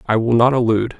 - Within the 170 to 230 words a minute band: No, fast, 240 wpm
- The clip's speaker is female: No, male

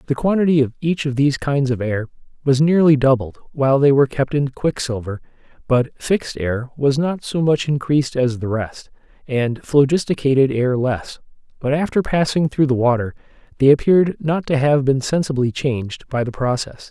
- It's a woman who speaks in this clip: No, male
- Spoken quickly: No, average, 175 wpm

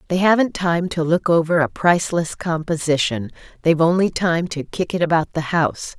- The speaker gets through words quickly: No, average, 180 wpm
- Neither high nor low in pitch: Yes, medium, 165 Hz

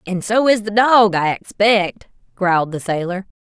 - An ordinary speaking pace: Yes, average, 175 wpm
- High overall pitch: Yes, high, 200 Hz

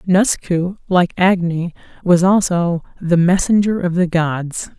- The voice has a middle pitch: Yes, medium, 180 Hz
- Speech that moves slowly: Yes, slow, 125 wpm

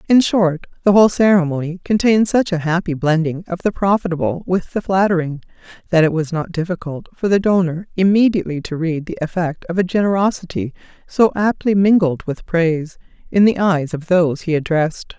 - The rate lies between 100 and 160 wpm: No, average, 175 wpm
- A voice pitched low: No, medium, 180 Hz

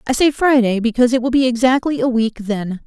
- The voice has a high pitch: Yes, high, 240 Hz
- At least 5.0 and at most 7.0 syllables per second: Yes, 6.0 syllables/s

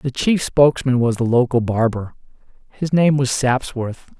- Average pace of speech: Yes, average, 155 wpm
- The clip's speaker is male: Yes, male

